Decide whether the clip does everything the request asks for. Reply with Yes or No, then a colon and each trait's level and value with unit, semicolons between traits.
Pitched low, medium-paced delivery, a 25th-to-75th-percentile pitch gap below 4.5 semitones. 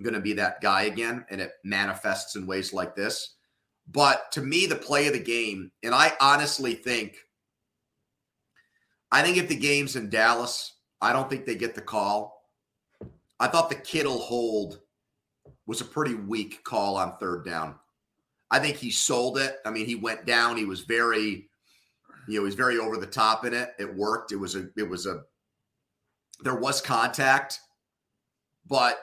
Yes: low, 110 Hz; average, 180 wpm; average, 2.8 semitones